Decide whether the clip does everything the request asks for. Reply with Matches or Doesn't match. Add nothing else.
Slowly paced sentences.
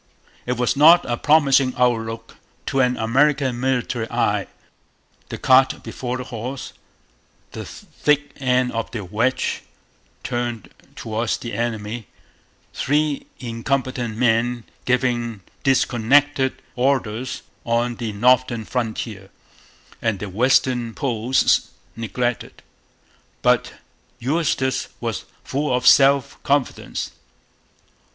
Matches